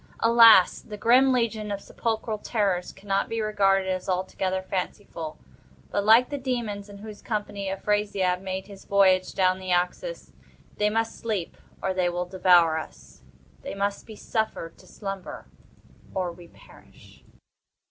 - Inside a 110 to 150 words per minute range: Yes, average, 140 wpm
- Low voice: No, high, 195 Hz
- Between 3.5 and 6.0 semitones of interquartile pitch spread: No, average, 2.8 semitones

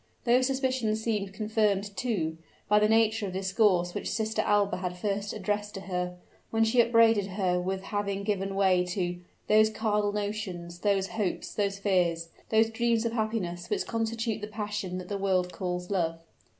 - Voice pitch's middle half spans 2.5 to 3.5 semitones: Yes, average, 2.9 semitones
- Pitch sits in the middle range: No, high, 205 Hz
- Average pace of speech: Yes, average, 175 wpm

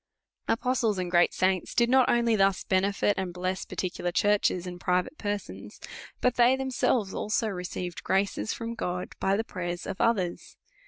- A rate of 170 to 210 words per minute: No, average, 160 wpm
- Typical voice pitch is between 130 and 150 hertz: No, high, 195 Hz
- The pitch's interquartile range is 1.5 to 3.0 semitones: No, average, 4.1 semitones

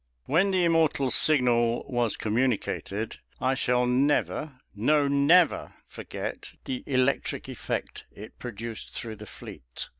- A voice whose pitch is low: Yes, low, 125 Hz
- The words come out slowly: Yes, slow, 120 wpm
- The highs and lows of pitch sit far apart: No, average, 3.8 semitones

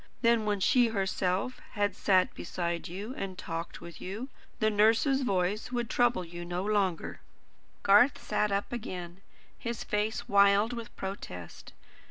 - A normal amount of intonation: Yes, average, 3.6 semitones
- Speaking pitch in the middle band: No, high, 200 Hz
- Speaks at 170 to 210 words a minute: No, average, 145 wpm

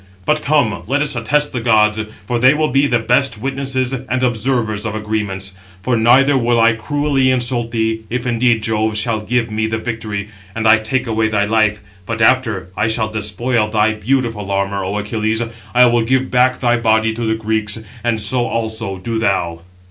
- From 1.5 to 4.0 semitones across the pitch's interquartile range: Yes, narrow, 2.5 semitones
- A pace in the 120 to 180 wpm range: No, average, 190 wpm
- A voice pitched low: Yes, low, 115 Hz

